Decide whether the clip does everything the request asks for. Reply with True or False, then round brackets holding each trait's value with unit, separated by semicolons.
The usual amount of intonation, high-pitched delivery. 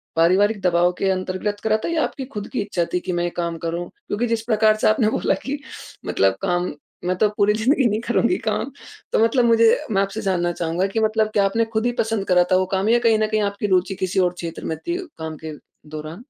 True (3.8 semitones; 200 Hz)